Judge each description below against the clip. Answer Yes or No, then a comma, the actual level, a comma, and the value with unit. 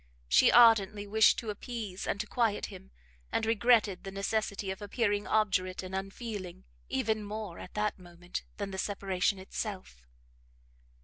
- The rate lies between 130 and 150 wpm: Yes, average, 145 wpm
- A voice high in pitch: Yes, high, 205 Hz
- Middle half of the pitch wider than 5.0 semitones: No, narrow, 2.4 semitones